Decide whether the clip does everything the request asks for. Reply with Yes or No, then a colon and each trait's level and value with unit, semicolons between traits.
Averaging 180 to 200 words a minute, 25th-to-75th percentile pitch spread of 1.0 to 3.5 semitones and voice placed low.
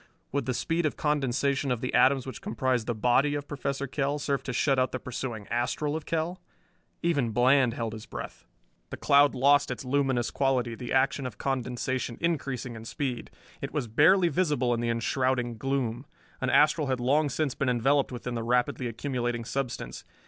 Yes: average, 185 wpm; average, 2.8 semitones; low, 130 Hz